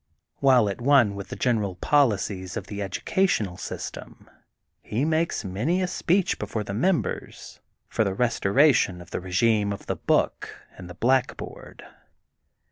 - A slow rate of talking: No, average, 160 wpm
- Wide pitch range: Yes, wide, 6.0 semitones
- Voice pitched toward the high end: No, low, 110 Hz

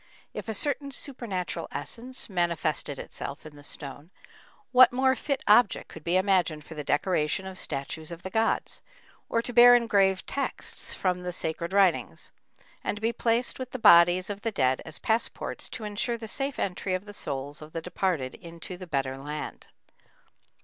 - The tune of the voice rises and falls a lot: Yes, wide, 6.2 semitones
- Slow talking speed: No, average, 175 wpm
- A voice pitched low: No, medium, 185 Hz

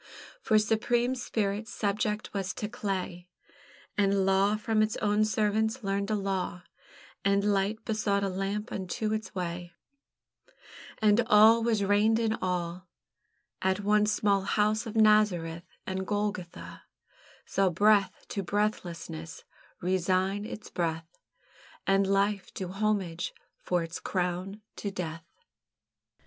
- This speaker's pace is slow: Yes, slow, 125 wpm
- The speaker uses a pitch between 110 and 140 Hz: No, high, 200 Hz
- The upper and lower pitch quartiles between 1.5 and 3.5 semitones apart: Yes, narrow, 2.4 semitones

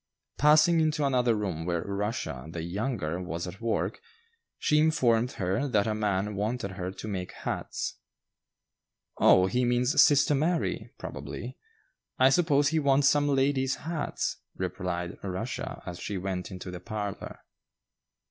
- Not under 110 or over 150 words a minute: Yes, average, 140 wpm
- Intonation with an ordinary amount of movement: No, wide, 7.1 semitones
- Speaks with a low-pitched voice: Yes, low, 110 Hz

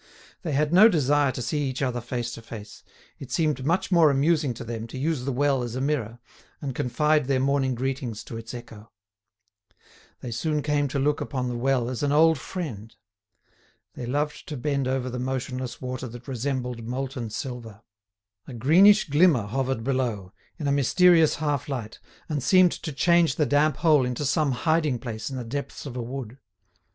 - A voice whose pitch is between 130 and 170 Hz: Yes, low, 135 Hz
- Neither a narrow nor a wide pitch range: Yes, average, 3.5 semitones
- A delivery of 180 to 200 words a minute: Yes, average, 185 wpm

